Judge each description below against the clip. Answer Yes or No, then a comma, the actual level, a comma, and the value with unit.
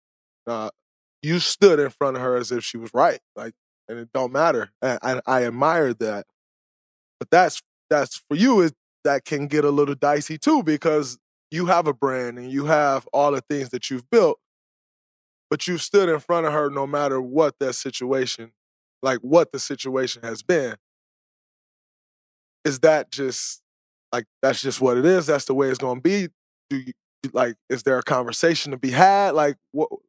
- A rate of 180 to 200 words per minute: Yes, average, 190 wpm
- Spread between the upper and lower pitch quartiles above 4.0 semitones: No, average, 3.7 semitones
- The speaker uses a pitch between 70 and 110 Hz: No, medium, 140 Hz